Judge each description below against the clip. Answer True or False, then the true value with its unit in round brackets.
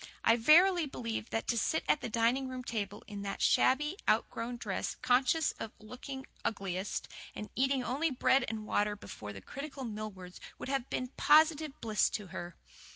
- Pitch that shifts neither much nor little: True (4.4 semitones)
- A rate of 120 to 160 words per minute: False (175 wpm)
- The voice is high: True (240 Hz)